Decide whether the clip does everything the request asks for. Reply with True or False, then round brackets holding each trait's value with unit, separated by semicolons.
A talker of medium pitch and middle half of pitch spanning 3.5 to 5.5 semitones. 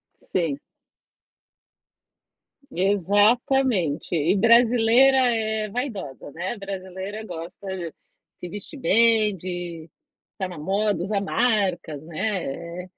False (195 Hz; 4.2 semitones)